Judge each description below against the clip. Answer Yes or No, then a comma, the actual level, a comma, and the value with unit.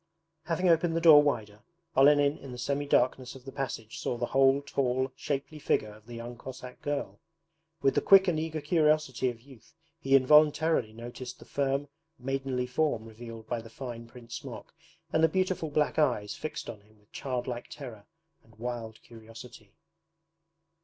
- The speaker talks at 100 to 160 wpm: No, average, 170 wpm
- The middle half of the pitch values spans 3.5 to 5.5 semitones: Yes, average, 3.9 semitones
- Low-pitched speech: Yes, low, 130 Hz